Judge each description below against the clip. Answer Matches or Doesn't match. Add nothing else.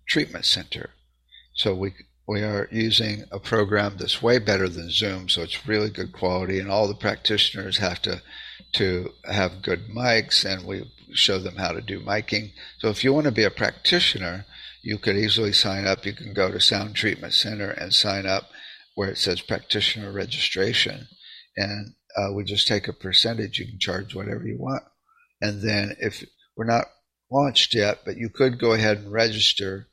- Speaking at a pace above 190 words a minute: Doesn't match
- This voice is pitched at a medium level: Doesn't match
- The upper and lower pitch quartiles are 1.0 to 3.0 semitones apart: Matches